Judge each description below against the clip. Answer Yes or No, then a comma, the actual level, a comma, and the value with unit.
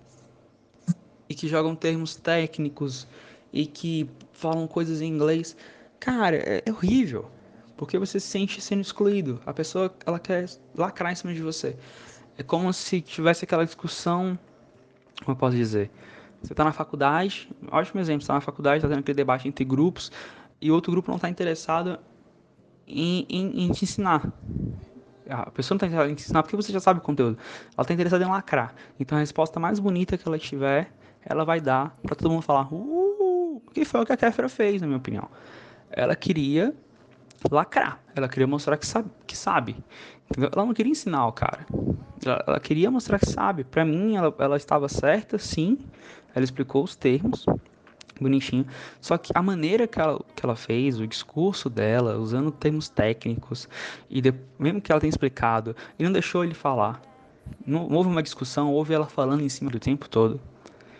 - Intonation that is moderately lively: Yes, average, 4.9 semitones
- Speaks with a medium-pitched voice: Yes, medium, 155 Hz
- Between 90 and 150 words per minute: No, average, 180 wpm